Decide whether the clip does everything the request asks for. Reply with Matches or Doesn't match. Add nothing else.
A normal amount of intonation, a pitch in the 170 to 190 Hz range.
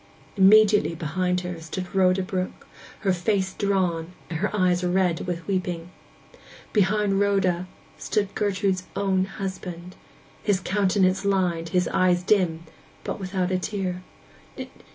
Doesn't match